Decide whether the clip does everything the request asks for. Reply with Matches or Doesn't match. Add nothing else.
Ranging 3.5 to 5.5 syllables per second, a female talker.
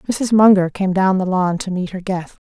Matches